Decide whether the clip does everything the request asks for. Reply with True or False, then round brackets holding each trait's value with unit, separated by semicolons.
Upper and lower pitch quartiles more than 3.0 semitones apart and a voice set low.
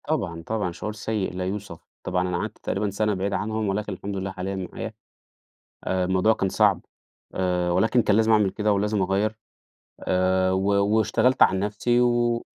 False (2.7 semitones; 100 Hz)